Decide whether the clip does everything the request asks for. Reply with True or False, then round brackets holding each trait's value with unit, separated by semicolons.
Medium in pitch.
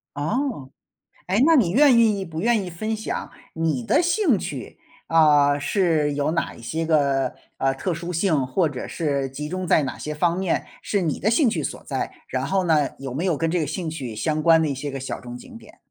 True (160 Hz)